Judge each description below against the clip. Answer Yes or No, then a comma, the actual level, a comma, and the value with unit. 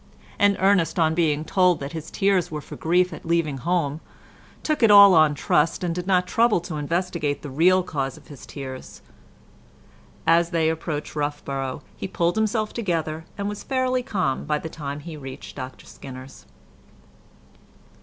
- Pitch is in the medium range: Yes, medium, 165 Hz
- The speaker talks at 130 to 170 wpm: Yes, average, 165 wpm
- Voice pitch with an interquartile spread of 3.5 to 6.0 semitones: Yes, average, 4.0 semitones